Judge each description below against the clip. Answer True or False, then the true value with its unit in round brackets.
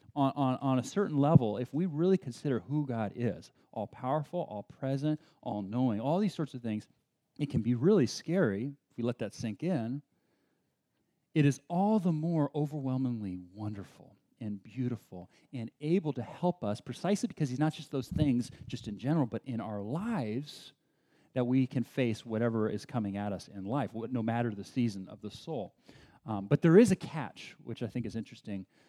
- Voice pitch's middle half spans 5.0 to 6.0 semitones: True (5.3 semitones)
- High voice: False (130 Hz)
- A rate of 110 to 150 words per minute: False (195 wpm)